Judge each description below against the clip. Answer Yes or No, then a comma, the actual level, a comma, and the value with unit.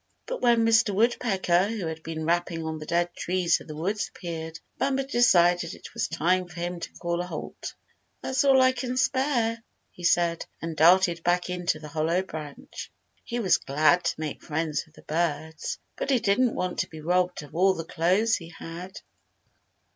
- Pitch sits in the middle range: Yes, medium, 175 Hz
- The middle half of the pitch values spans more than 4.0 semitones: Yes, average, 4.7 semitones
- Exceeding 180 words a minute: Yes, average, 190 wpm